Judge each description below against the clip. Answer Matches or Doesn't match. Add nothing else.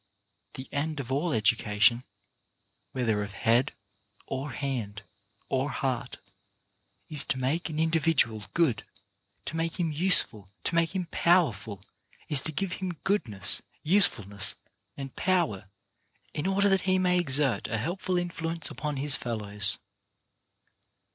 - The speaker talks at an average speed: Doesn't match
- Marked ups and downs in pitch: Matches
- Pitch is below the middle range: Doesn't match